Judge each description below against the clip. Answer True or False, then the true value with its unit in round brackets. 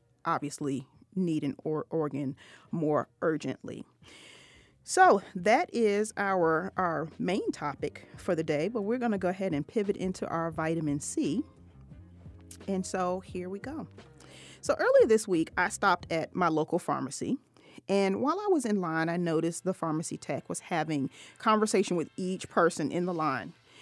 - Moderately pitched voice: True (170 Hz)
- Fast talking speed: False (160 wpm)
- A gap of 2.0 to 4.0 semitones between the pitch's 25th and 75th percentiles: False (4.9 semitones)